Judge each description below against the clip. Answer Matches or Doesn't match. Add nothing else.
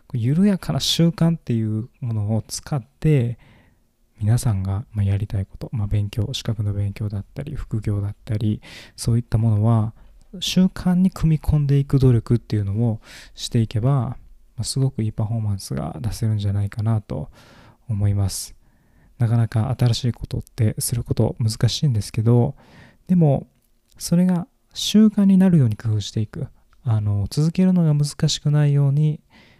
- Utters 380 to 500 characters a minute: Doesn't match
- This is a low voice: Matches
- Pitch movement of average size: Matches